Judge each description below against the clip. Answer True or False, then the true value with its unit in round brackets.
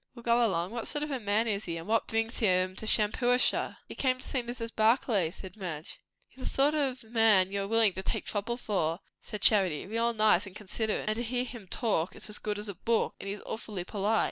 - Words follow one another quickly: True (245 wpm)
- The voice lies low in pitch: False (215 Hz)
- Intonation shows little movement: False (3.3 semitones)